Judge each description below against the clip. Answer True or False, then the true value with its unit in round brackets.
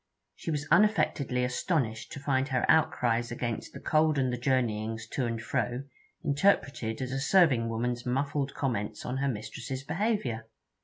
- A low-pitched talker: True (130 Hz)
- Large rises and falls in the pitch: False (3.5 semitones)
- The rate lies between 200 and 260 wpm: False (155 wpm)